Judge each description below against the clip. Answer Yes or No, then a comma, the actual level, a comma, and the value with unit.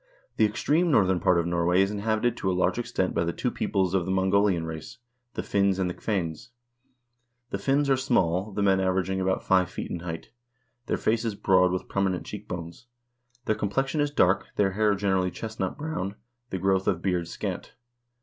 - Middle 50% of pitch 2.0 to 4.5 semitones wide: Yes, average, 2.9 semitones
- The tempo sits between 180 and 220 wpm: Yes, average, 195 wpm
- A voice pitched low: Yes, very low, 95 Hz